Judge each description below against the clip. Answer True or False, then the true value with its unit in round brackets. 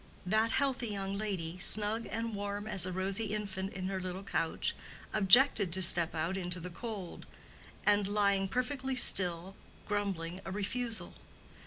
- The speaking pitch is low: False (200 Hz)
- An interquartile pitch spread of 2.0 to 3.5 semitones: True (2.6 semitones)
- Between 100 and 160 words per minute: True (150 wpm)